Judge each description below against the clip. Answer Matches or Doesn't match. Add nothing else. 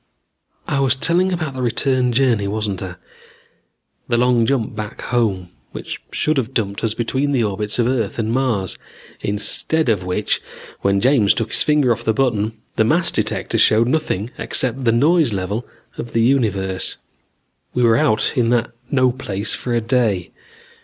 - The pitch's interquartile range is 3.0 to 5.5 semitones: Matches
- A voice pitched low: Matches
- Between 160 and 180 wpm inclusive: Matches